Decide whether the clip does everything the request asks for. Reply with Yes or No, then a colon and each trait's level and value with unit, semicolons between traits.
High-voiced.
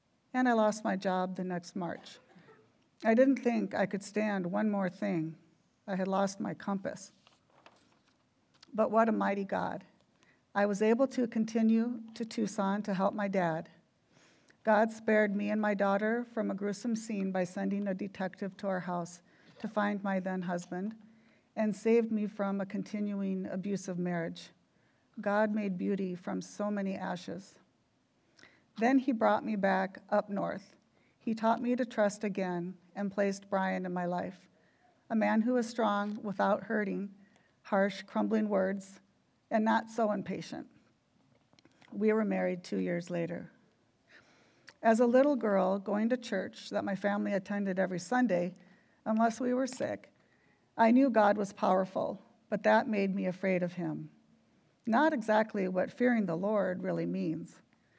Yes: high, 205 Hz